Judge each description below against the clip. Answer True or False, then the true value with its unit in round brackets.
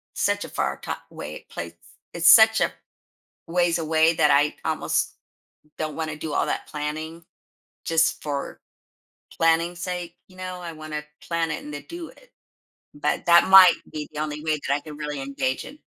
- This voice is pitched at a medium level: True (160 Hz)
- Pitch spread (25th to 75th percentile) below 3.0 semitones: True (2.4 semitones)